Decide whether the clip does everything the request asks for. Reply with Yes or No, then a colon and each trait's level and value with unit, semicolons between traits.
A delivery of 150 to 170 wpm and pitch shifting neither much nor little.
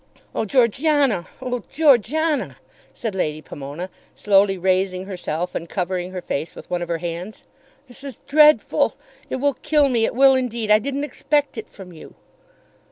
No: average, 165 wpm; wide, 7.2 semitones